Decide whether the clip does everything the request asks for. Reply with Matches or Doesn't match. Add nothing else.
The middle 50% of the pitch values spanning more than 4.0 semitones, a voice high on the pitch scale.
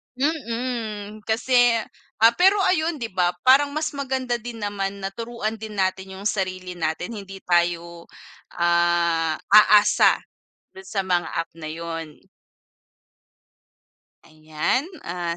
Matches